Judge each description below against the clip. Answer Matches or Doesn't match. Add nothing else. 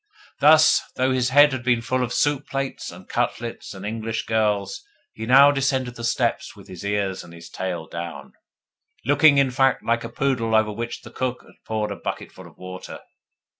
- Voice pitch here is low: Matches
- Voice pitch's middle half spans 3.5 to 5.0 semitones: Matches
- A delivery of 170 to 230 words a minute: Matches